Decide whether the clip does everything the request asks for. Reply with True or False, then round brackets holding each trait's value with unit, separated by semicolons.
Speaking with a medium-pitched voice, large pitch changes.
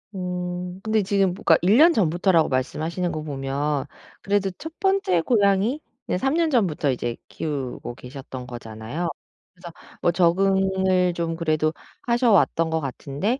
False (175 Hz; 4.6 semitones)